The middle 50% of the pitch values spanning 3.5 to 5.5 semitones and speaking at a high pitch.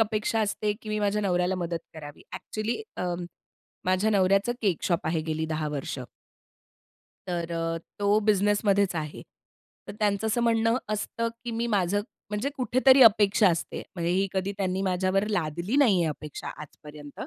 Yes: average, 3.8 semitones; high, 195 Hz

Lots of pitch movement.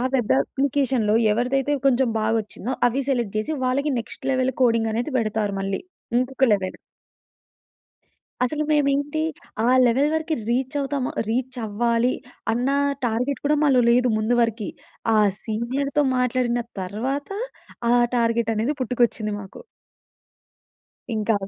No: average, 3.3 semitones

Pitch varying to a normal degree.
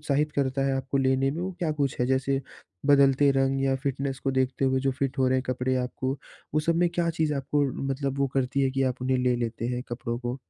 No: narrow, 1.2 semitones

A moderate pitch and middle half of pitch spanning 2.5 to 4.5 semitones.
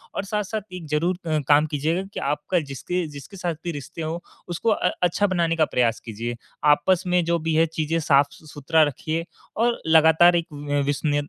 Yes: medium, 160 Hz; average, 3.2 semitones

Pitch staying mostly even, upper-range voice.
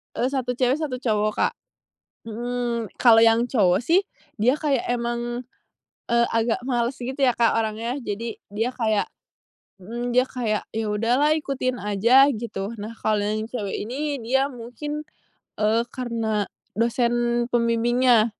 Yes: narrow, 2.3 semitones; high, 235 Hz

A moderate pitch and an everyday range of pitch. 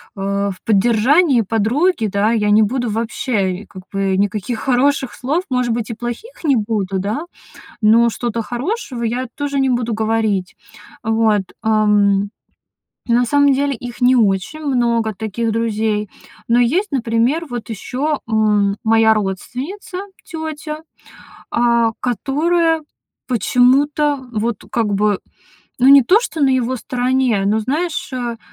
No: high, 235 Hz; average, 4.0 semitones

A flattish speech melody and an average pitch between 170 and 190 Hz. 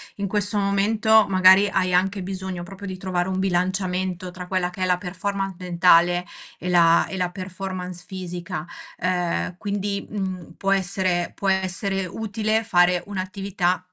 Yes: narrow, 1.5 semitones; medium, 185 Hz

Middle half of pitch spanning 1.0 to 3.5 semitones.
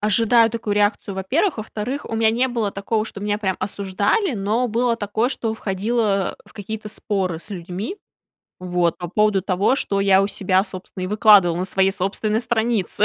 Yes: average, 2.8 semitones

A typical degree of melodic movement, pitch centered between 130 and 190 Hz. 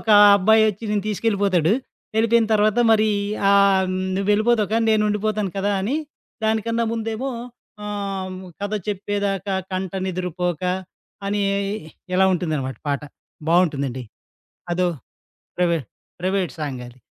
No: average, 3.1 semitones; high, 200 Hz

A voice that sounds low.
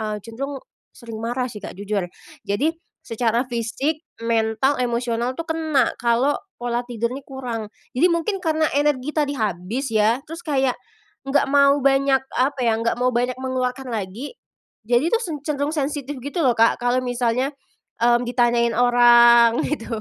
No: high, 245 Hz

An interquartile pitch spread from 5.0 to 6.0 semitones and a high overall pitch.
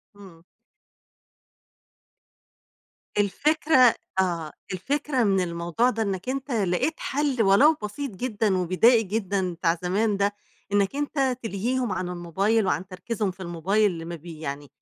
Yes: average, 5.3 semitones; high, 200 Hz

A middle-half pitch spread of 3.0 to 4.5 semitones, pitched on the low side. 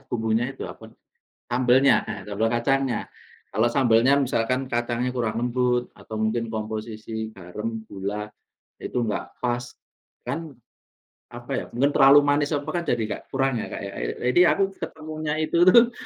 Yes: average, 3.9 semitones; low, 120 Hz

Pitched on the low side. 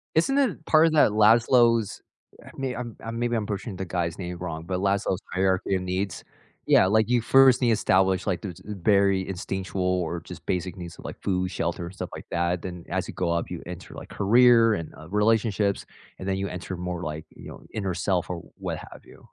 Yes: very low, 95 Hz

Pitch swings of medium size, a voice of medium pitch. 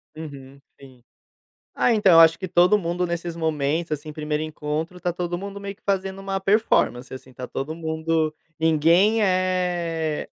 Yes: average, 3.2 semitones; medium, 165 Hz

